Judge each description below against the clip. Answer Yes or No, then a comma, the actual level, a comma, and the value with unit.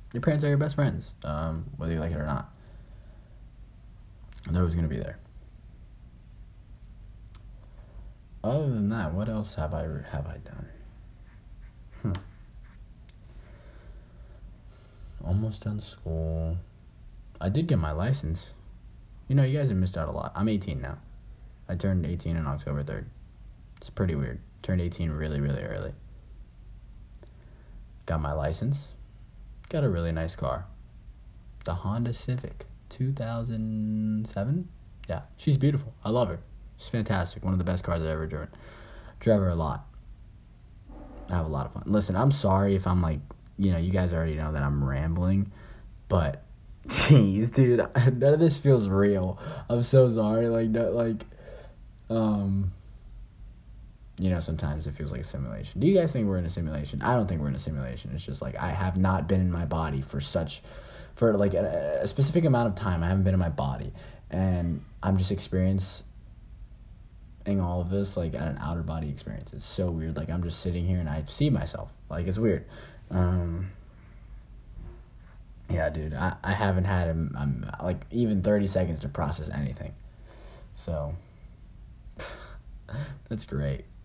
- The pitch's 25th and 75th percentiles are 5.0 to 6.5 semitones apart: Yes, average, 5.3 semitones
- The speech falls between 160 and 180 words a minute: Yes, average, 165 wpm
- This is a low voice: Yes, very low, 95 Hz